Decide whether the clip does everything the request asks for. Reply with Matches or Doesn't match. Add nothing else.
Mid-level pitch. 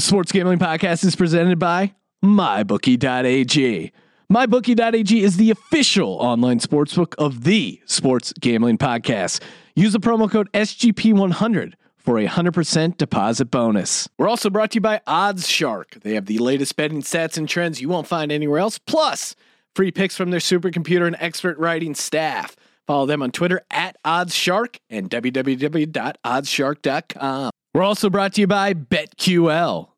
Matches